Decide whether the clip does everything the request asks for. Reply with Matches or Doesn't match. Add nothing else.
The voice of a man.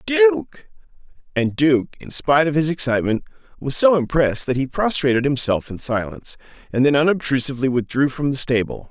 Matches